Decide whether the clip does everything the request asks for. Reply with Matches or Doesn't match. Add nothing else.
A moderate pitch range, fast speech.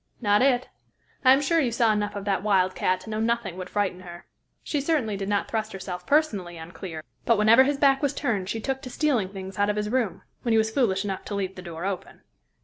Matches